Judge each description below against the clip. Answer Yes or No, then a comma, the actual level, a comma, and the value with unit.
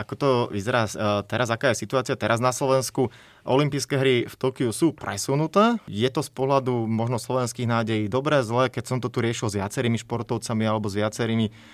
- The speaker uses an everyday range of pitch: Yes, average, 3.0 semitones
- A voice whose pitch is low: Yes, low, 125 Hz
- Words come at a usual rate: No, fast, 185 wpm